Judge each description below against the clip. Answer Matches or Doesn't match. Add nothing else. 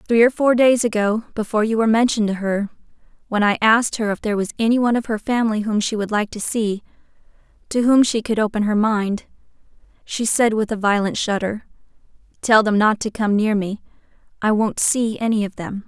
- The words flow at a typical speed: Matches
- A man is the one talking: Doesn't match